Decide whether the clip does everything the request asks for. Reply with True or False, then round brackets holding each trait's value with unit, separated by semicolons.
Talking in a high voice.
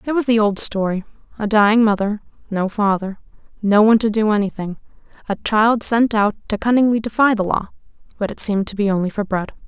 True (210 Hz)